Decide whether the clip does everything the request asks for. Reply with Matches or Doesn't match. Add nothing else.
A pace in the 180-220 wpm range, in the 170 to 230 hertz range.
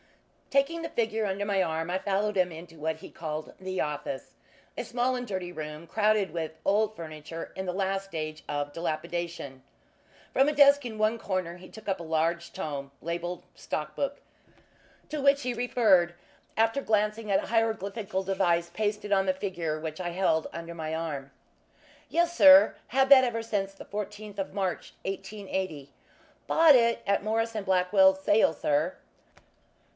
Doesn't match